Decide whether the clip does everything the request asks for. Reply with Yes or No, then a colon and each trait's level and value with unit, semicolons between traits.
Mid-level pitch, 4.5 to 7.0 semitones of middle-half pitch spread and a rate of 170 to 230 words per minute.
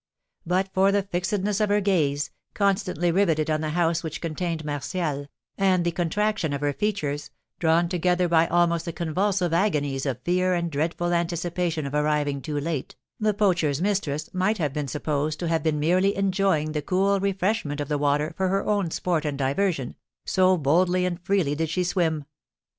No: medium, 170 Hz; average, 3.9 semitones; average, 180 wpm